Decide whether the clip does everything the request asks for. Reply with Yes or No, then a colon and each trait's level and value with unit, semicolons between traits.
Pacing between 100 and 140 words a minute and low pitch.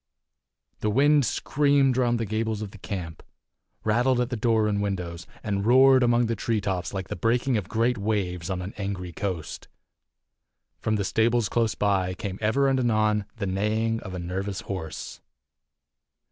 No: average, 170 wpm; low, 105 Hz